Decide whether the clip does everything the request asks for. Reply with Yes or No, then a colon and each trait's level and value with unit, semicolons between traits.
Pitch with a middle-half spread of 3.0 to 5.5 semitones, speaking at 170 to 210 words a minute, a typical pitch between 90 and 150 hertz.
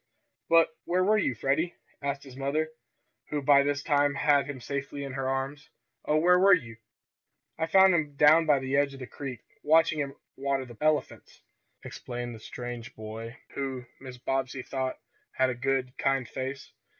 No: narrow, 2.4 semitones; average, 175 wpm; medium, 140 Hz